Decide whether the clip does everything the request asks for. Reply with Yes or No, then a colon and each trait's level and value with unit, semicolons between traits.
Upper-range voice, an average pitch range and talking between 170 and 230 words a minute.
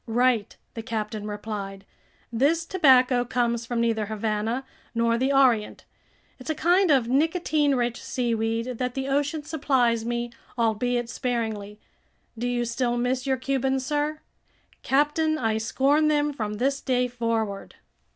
No: high, 245 Hz; average, 3.3 semitones; average, 140 wpm